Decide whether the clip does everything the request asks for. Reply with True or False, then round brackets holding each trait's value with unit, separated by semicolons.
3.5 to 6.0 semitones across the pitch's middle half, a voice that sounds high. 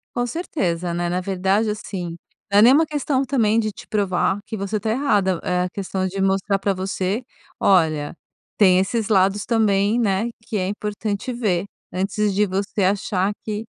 False (2.6 semitones; 200 Hz)